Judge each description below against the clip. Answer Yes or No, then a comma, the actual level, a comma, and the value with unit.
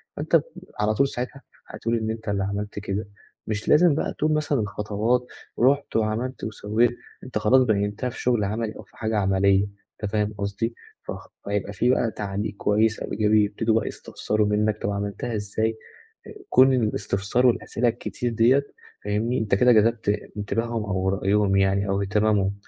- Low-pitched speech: Yes, low, 110 Hz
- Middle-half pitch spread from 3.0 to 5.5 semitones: No, narrow, 2.4 semitones